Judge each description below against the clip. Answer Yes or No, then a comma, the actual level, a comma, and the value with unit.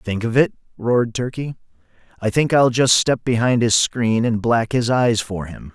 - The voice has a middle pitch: No, low, 115 Hz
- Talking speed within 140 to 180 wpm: No, average, 200 wpm